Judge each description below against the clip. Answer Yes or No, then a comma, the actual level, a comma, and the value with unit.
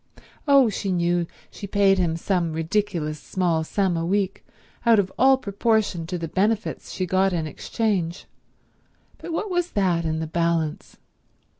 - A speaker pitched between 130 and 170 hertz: No, medium, 185 Hz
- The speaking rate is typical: Yes, average, 155 wpm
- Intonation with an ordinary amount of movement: Yes, average, 3.7 semitones